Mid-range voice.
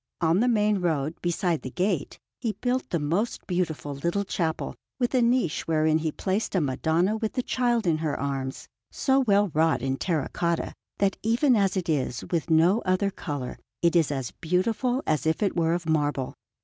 Yes: medium, 175 Hz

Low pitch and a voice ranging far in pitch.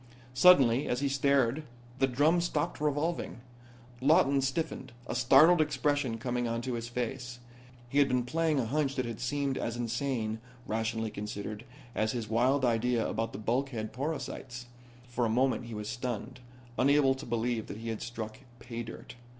No: low, 125 Hz; average, 3.2 semitones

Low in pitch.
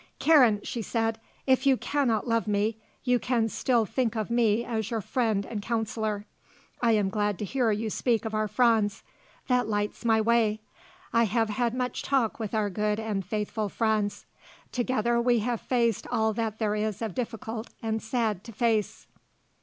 No: high, 225 Hz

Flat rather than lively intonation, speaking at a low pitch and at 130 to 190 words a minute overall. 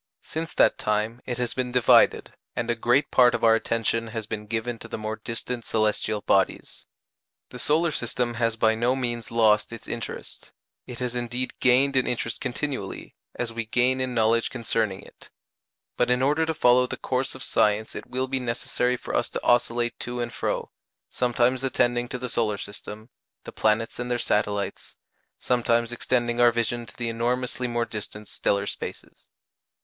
Yes: narrow, 1.8 semitones; low, 120 Hz; average, 180 wpm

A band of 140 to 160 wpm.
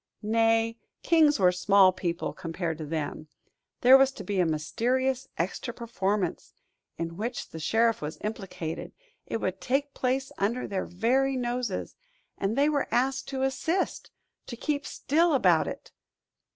Yes: average, 150 wpm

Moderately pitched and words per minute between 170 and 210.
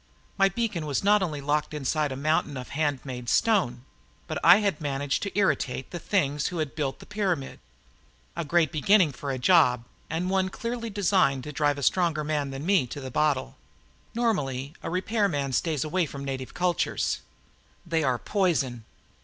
Yes: medium, 155 Hz; average, 175 wpm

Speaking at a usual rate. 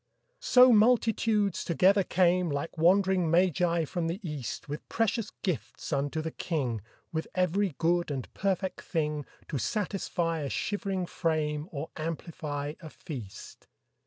No: slow, 130 wpm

